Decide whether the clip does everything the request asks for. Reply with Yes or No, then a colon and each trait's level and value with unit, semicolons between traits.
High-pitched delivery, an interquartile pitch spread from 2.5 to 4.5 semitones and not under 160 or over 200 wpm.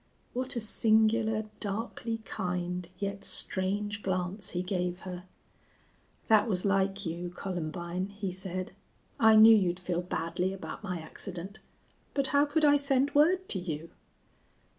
No: high, 195 Hz; average, 3.6 semitones; average, 140 wpm